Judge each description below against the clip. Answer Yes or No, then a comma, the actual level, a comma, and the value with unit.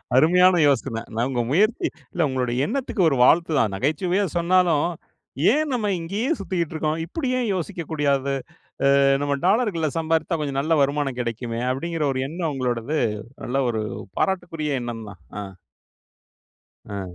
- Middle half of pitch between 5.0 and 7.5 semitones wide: Yes, average, 5.3 semitones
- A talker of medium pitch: Yes, medium, 155 Hz